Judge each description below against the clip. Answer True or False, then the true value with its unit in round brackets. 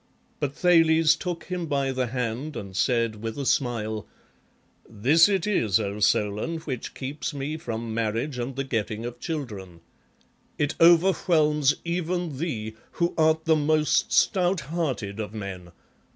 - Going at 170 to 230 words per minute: False (150 wpm)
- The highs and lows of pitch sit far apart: True (6.5 semitones)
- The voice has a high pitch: False (135 Hz)